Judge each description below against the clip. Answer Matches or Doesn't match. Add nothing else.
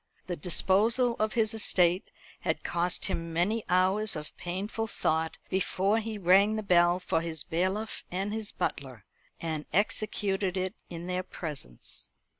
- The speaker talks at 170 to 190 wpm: Doesn't match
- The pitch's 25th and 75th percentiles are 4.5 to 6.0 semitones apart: Doesn't match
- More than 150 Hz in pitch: Matches